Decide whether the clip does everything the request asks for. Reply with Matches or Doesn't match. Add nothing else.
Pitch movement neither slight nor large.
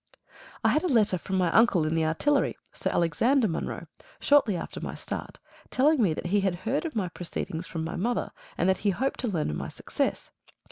Doesn't match